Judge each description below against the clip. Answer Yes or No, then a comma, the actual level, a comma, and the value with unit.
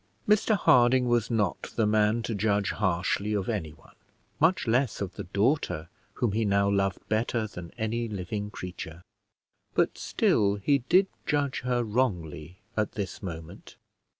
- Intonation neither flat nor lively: Yes, average, 3.9 semitones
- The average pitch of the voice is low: Yes, low, 105 Hz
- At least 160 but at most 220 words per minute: No, average, 150 wpm